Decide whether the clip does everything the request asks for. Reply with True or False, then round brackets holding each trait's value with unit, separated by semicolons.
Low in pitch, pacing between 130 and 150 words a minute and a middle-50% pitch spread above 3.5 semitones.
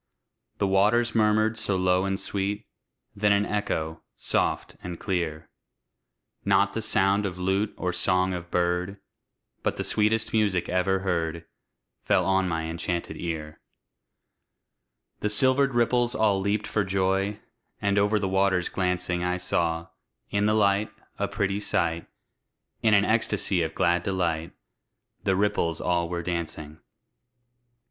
False (95 Hz; 140 wpm; 2.9 semitones)